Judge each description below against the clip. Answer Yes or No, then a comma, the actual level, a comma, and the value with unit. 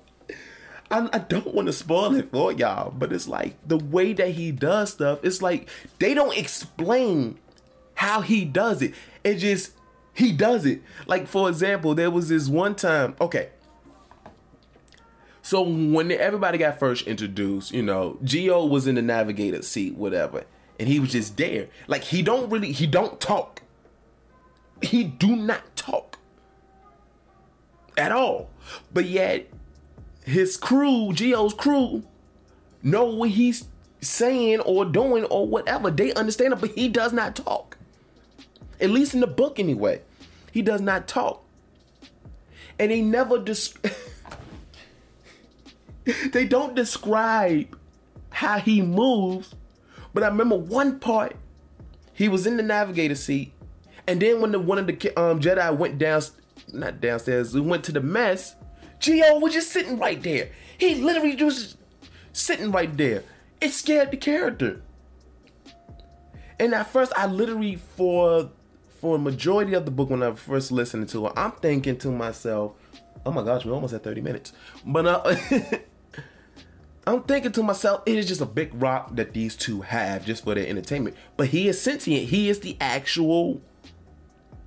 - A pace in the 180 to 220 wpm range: No, average, 155 wpm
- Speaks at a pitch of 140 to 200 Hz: Yes, medium, 185 Hz